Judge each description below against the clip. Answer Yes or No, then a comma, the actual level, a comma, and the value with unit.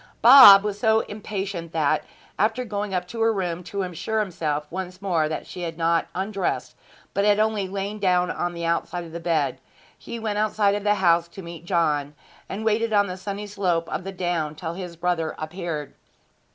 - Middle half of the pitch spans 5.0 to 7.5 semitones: No, average, 3.5 semitones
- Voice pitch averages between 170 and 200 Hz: Yes, medium, 185 Hz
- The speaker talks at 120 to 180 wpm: No, average, 195 wpm